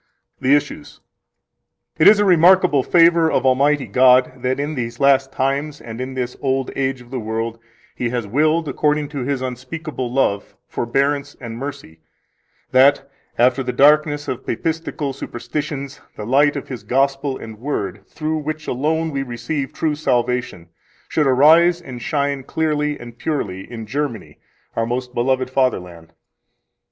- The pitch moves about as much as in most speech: Yes, average, 3.3 semitones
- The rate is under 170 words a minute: Yes, average, 155 wpm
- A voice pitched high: No, low, 135 Hz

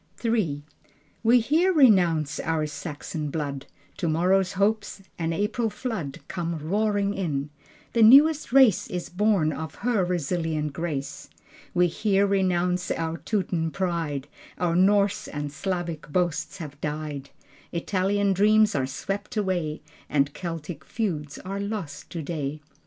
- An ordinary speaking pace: No, slow, 125 wpm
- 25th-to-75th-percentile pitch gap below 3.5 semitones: No, average, 4.8 semitones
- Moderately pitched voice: Yes, medium, 175 Hz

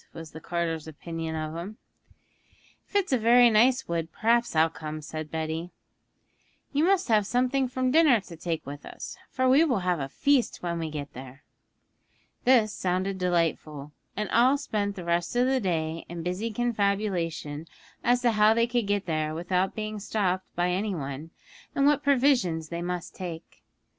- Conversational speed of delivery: Yes, average, 175 wpm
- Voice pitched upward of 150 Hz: Yes, medium, 185 Hz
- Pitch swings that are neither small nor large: No, wide, 6.6 semitones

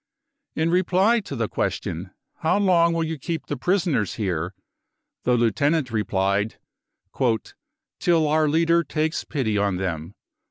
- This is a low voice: No, medium, 145 Hz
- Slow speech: No, average, 150 wpm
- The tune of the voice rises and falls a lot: Yes, wide, 8.2 semitones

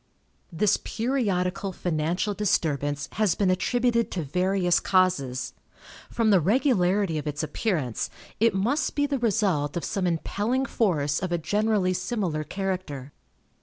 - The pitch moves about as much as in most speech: Yes, average, 4.9 semitones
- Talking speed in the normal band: No, slow, 130 wpm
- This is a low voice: No, medium, 185 Hz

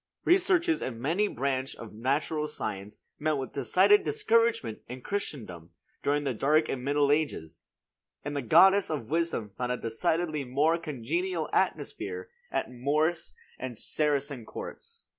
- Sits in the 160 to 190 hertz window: No, medium, 145 Hz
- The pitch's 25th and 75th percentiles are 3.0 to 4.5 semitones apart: No, average, 5.2 semitones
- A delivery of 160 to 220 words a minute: No, average, 140 wpm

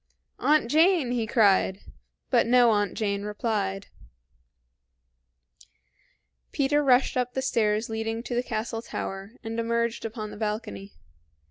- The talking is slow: Yes, slow, 125 wpm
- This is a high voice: Yes, high, 225 Hz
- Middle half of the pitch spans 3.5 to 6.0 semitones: No, average, 2.8 semitones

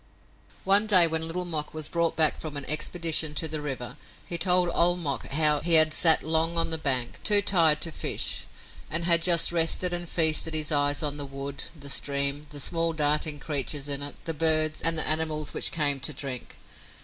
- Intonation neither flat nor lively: No, narrow, 2.3 semitones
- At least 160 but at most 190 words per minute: No, fast, 205 wpm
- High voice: No, medium, 155 Hz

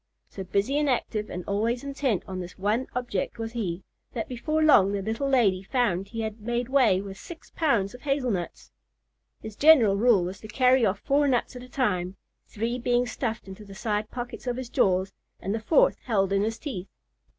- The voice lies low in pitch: No, high, 225 Hz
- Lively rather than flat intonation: No, average, 4.2 semitones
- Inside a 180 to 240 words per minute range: Yes, average, 200 wpm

